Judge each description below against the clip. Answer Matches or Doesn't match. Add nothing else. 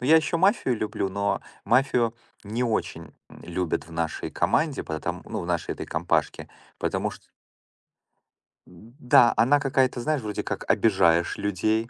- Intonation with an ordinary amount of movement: Doesn't match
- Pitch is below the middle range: Matches